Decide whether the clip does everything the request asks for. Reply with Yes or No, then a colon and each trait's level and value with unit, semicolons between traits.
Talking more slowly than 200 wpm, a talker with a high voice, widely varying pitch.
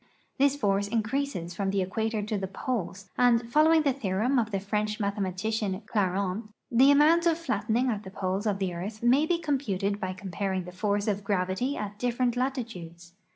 No: average, 185 wpm; high, 210 Hz; average, 4.4 semitones